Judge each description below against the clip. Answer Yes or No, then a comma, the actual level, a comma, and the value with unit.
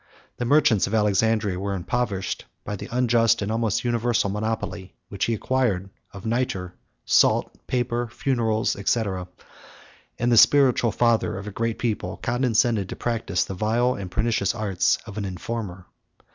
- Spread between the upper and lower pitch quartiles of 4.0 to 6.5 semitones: No, average, 3.3 semitones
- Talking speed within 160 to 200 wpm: No, average, 150 wpm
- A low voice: Yes, low, 110 Hz